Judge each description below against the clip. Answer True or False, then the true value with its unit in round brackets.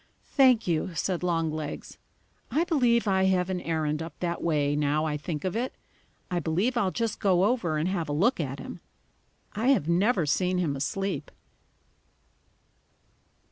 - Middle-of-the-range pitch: True (180 Hz)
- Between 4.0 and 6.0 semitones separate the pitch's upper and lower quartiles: True (5.1 semitones)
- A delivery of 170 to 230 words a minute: False (160 wpm)